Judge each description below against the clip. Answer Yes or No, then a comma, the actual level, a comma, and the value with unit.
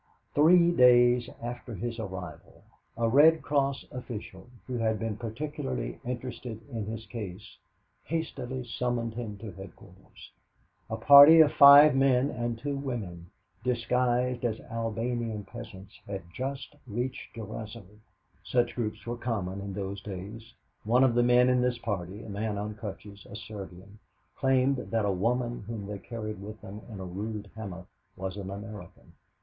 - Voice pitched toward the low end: Yes, low, 115 Hz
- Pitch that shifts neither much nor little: Yes, average, 3.5 semitones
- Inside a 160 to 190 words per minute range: No, average, 150 wpm